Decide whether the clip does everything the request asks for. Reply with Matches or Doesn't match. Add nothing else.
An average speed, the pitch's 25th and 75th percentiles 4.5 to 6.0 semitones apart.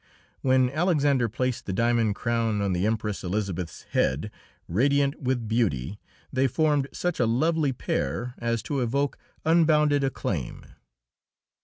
Doesn't match